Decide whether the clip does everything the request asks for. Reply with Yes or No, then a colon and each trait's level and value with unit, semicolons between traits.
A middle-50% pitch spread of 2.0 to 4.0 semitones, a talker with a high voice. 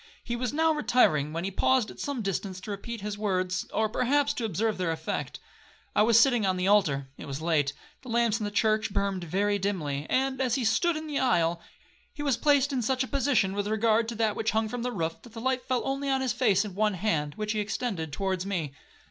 No: average, 5.1 semitones; high, 215 Hz